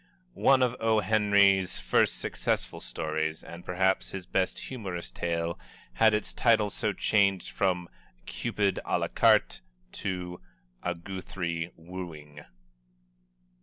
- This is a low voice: Yes, very low, 95 Hz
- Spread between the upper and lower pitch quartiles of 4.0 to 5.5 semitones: No, average, 3.2 semitones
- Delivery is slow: Yes, slow, 120 wpm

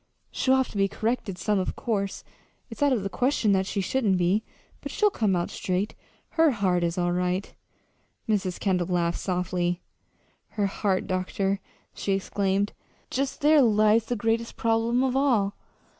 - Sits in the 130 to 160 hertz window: No, high, 200 Hz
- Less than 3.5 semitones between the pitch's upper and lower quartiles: No, average, 3.8 semitones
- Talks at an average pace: Yes, average, 165 wpm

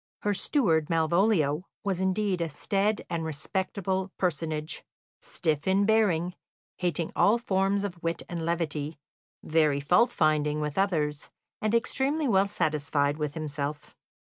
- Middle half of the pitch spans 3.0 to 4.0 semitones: No, average, 4.5 semitones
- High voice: No, medium, 170 Hz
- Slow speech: Yes, slow, 130 wpm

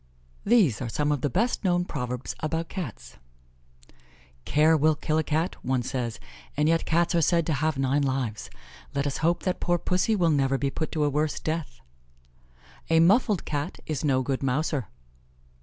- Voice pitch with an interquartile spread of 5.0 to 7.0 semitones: No, average, 3.7 semitones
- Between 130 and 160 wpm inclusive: No, average, 185 wpm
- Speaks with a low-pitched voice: No, medium, 155 Hz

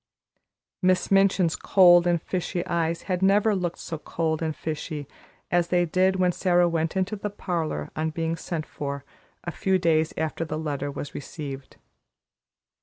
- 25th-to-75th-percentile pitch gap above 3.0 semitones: No, narrow, 2.6 semitones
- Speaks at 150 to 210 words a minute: Yes, average, 160 wpm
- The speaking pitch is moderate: Yes, medium, 170 Hz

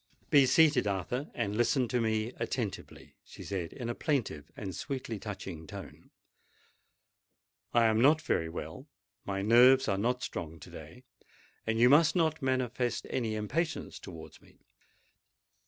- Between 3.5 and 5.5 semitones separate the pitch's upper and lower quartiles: Yes, average, 4.7 semitones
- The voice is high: No, low, 120 Hz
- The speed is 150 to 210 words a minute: No, slow, 135 wpm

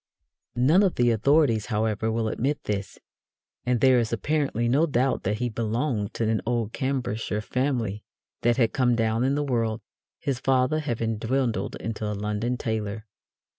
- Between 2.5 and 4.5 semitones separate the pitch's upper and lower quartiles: Yes, average, 3.1 semitones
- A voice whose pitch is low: Yes, low, 120 Hz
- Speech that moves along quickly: No, average, 165 wpm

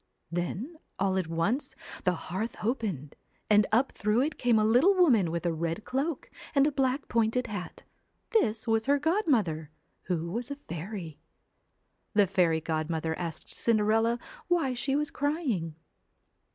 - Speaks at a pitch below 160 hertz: No, high, 220 Hz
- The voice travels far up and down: Yes, wide, 7.7 semitones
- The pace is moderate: Yes, average, 150 wpm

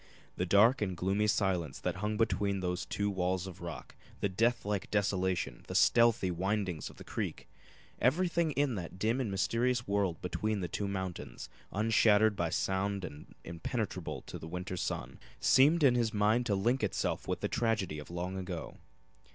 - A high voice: No, low, 100 Hz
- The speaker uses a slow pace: No, average, 175 wpm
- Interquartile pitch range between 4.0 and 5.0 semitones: No, average, 3.6 semitones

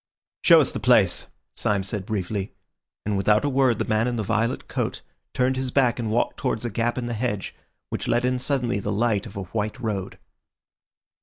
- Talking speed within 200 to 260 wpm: Yes, fast, 205 wpm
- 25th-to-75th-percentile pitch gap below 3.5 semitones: Yes, average, 2.9 semitones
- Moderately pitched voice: No, low, 115 Hz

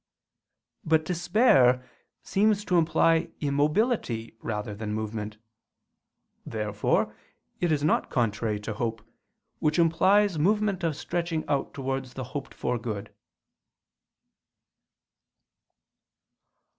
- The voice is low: No, medium, 145 Hz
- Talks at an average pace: No, slow, 95 wpm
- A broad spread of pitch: Yes, wide, 7.2 semitones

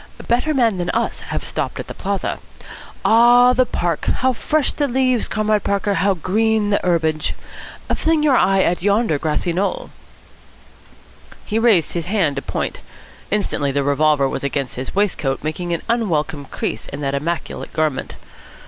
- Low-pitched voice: No, high, 190 Hz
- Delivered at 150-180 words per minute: Yes, average, 160 wpm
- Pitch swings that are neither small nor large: No, wide, 6.8 semitones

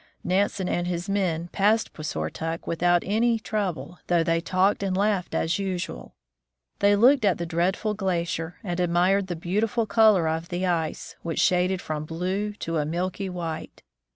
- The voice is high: No, medium, 180 Hz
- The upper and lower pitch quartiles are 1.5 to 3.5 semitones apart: Yes, average, 3.1 semitones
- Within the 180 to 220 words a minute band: No, average, 160 wpm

